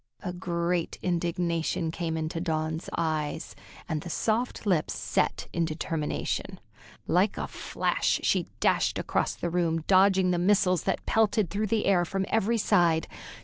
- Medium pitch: Yes, medium, 175 Hz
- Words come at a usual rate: Yes, average, 145 wpm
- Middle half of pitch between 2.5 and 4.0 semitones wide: Yes, average, 2.8 semitones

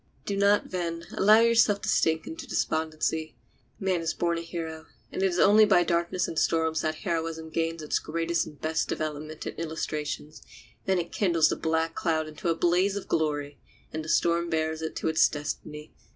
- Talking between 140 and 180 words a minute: No, average, 190 wpm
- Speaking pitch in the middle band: Yes, medium, 165 Hz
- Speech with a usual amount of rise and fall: No, narrow, 1.8 semitones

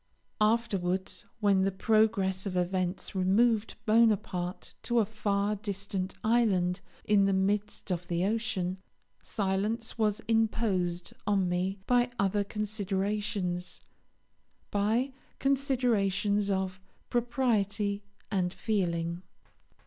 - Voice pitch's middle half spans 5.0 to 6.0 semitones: No, average, 2.8 semitones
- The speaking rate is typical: No, slow, 100 wpm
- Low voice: No, high, 200 Hz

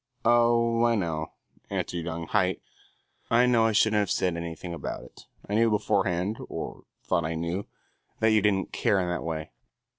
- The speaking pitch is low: Yes, very low, 95 Hz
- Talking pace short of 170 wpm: No, average, 175 wpm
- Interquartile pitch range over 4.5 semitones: Yes, average, 4.9 semitones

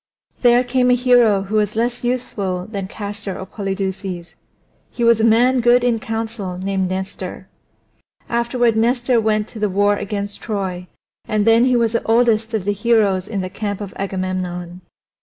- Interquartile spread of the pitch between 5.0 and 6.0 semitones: No, average, 3.4 semitones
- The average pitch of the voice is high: Yes, high, 215 Hz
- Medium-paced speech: Yes, average, 170 wpm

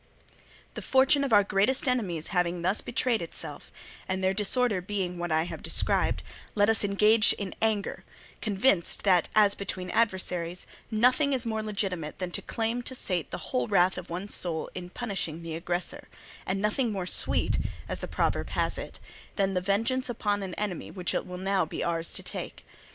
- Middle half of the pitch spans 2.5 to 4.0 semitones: Yes, average, 3.5 semitones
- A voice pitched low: No, high, 195 Hz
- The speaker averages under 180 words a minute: No, average, 185 wpm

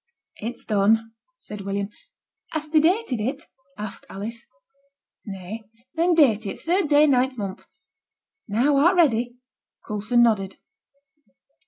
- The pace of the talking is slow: Yes, slow, 120 wpm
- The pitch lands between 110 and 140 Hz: No, high, 235 Hz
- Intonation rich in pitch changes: Yes, wide, 6.0 semitones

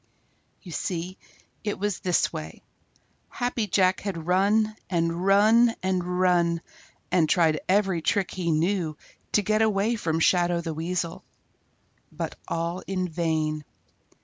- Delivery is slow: Yes, slow, 130 wpm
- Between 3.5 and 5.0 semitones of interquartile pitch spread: No, average, 3.1 semitones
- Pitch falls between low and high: Yes, medium, 180 Hz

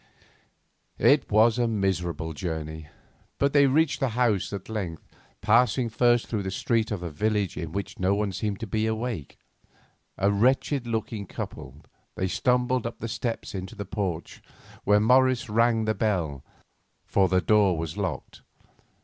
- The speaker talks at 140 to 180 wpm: Yes, average, 160 wpm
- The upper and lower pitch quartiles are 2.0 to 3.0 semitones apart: No, average, 4.0 semitones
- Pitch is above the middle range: No, low, 105 Hz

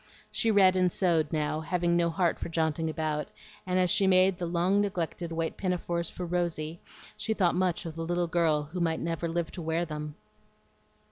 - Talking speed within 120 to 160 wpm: No, average, 195 wpm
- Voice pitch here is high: No, medium, 170 Hz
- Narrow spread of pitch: Yes, narrow, 2.0 semitones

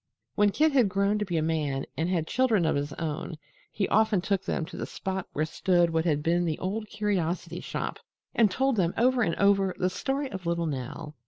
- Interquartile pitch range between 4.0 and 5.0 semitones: Yes, average, 4.3 semitones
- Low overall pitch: No, medium, 185 Hz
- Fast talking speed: Yes, fast, 220 wpm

